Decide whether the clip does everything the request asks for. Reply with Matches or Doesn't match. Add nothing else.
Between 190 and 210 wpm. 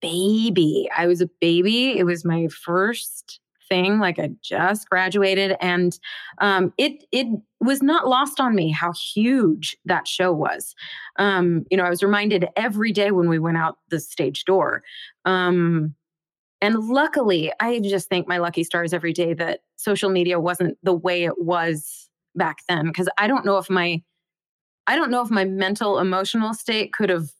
Doesn't match